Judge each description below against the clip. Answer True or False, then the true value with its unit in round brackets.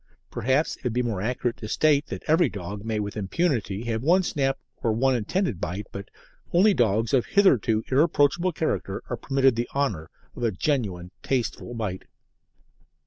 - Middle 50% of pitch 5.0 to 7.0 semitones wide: True (5.3 semitones)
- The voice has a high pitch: False (120 Hz)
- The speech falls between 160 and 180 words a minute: True (170 wpm)